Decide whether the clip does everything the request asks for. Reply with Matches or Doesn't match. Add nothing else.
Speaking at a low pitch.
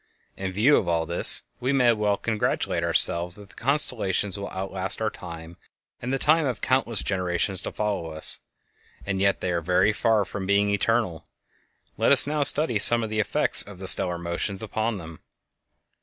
Matches